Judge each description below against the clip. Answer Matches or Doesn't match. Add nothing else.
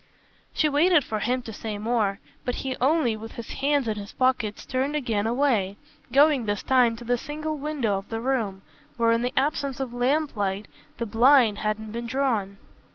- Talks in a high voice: Matches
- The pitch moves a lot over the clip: Doesn't match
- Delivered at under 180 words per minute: Doesn't match